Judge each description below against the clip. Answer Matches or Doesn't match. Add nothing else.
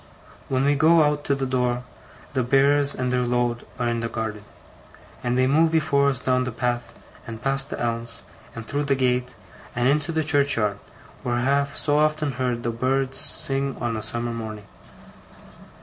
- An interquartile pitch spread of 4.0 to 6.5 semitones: Doesn't match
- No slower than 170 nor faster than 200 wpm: Matches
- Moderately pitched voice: Doesn't match